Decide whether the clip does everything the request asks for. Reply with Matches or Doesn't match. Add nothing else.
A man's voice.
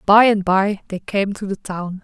Doesn't match